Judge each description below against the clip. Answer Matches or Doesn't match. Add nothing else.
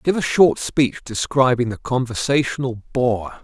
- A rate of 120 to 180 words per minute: Matches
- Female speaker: Doesn't match